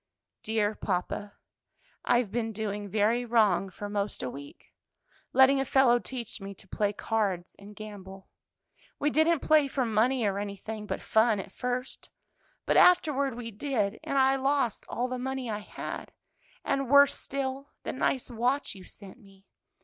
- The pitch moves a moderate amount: Yes, average, 4.5 semitones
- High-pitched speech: Yes, high, 225 Hz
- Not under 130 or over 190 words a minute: Yes, average, 160 wpm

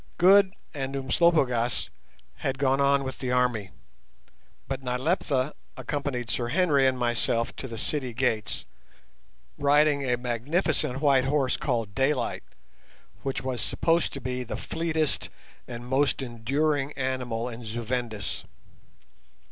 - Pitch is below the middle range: Yes, low, 130 Hz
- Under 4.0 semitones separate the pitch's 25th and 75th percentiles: Yes, average, 2.8 semitones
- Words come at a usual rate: No, slow, 125 wpm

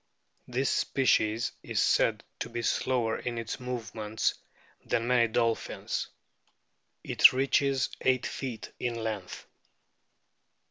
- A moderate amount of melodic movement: No, narrow, 2.2 semitones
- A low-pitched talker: Yes, low, 120 Hz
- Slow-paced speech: Yes, slow, 105 wpm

